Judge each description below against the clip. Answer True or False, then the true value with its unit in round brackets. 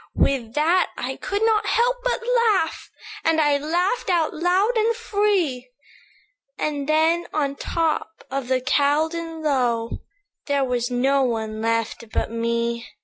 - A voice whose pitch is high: True (305 Hz)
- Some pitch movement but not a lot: False (6.4 semitones)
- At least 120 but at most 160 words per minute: True (145 wpm)